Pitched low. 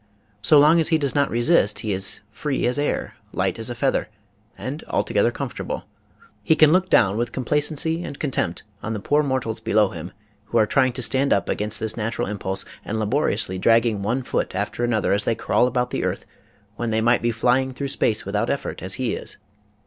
Yes: low, 120 Hz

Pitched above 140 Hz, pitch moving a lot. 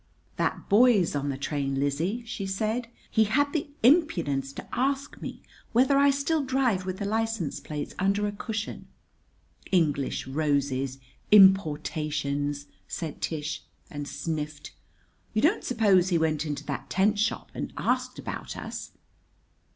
Yes: medium, 185 Hz; wide, 7.4 semitones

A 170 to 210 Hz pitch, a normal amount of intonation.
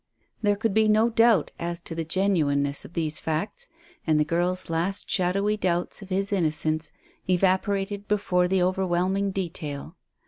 Yes: medium, 185 Hz; average, 3.4 semitones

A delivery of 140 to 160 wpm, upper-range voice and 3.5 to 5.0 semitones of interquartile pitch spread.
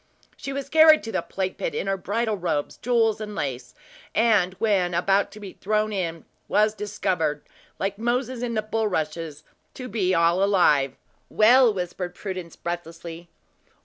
Yes: average, 155 wpm; high, 195 Hz; average, 4.2 semitones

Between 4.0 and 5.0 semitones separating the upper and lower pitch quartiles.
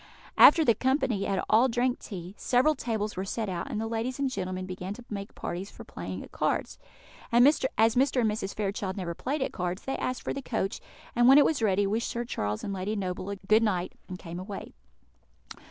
Yes: average, 4.5 semitones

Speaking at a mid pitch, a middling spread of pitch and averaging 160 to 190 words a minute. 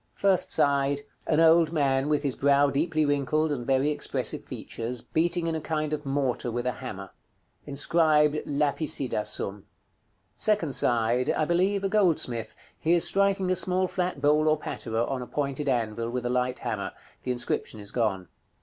Yes: medium, 145 Hz; average, 4.3 semitones; average, 170 wpm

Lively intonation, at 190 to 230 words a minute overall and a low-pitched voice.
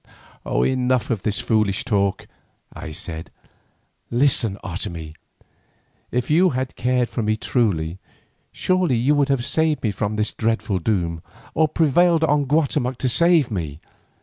No: wide, 6.3 semitones; average, 140 wpm; low, 120 Hz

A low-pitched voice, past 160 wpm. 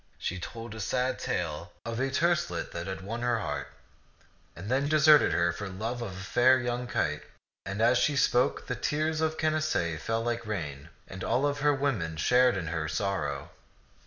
Yes: low, 115 Hz; average, 190 wpm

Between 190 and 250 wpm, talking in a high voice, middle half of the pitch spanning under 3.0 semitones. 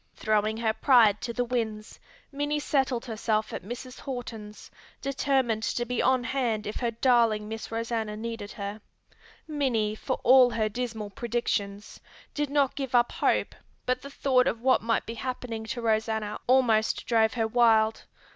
No: average, 160 wpm; high, 230 Hz; narrow, 2.6 semitones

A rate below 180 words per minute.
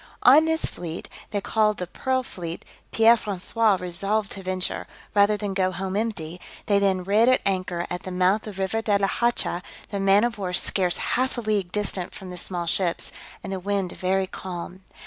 No: average, 195 wpm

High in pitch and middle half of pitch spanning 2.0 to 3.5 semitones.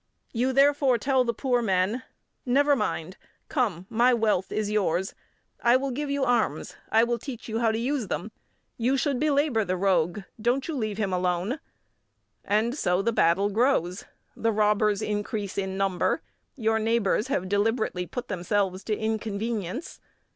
No: high, 220 Hz; average, 4.0 semitones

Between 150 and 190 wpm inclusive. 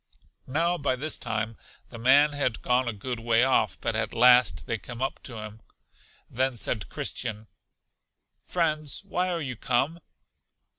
Yes: average, 155 wpm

